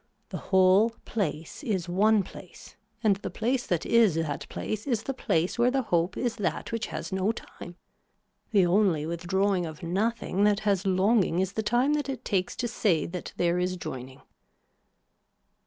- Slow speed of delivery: No, average, 170 wpm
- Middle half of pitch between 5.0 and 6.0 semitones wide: No, average, 4.3 semitones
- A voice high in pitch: Yes, high, 195 Hz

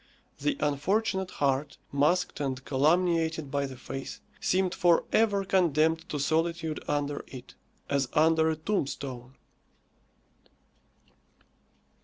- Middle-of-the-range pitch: Yes, medium, 155 Hz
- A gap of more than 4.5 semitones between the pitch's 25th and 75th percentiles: No, average, 4.0 semitones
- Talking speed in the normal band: No, slow, 105 wpm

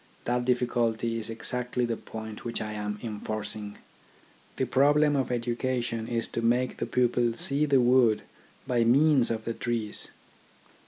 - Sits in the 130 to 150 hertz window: No, low, 120 Hz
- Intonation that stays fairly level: Yes, narrow, 1.9 semitones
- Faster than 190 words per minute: No, average, 150 wpm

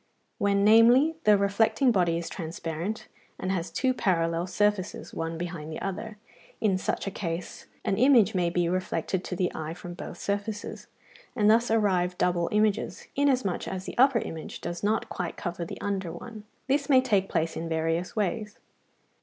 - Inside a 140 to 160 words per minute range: No, average, 170 wpm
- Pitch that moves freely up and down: No, average, 4.0 semitones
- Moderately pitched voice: No, high, 195 Hz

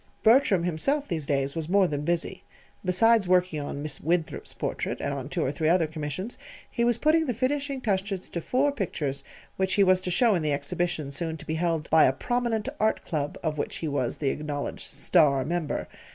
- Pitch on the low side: No, medium, 175 Hz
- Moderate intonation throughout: No, wide, 5.9 semitones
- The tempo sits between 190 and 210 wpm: Yes, fast, 205 wpm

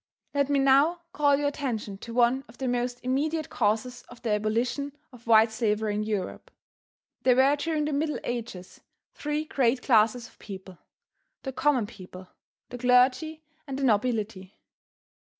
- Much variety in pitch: No, average, 4.3 semitones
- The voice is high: Yes, high, 245 Hz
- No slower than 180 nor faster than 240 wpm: No, average, 155 wpm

